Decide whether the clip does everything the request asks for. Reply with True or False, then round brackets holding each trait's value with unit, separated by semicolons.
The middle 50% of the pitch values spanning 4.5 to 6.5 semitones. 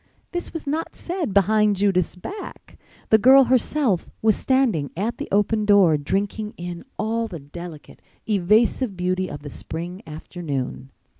True (4.8 semitones)